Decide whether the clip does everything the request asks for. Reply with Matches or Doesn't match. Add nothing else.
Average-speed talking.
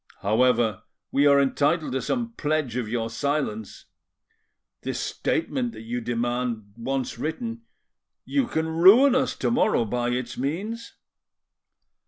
Doesn't match